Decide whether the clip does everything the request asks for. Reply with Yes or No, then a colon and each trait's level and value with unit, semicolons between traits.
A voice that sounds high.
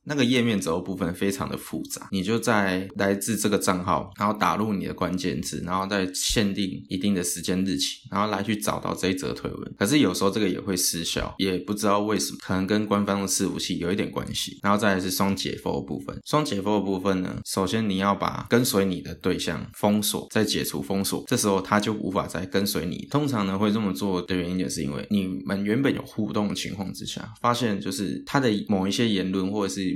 No: low, 100 Hz